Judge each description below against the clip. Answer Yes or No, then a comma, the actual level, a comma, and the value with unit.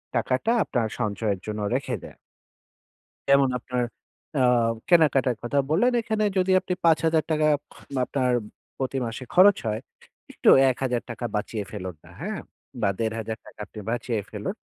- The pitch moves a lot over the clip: Yes, wide, 5.8 semitones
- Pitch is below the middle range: Yes, low, 125 Hz